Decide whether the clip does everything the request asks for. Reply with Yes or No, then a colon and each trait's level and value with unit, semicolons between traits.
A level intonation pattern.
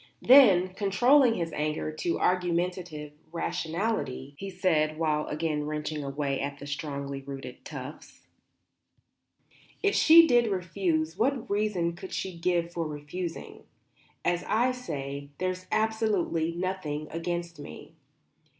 No: average, 4.2 semitones